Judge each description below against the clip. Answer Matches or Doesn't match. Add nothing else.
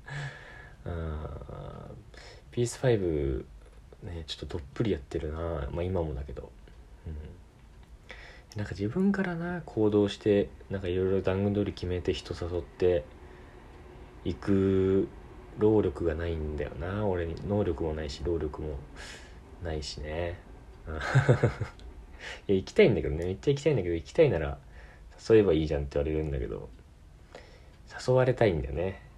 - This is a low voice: Matches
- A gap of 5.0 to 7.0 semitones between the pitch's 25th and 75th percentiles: Matches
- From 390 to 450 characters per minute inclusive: Doesn't match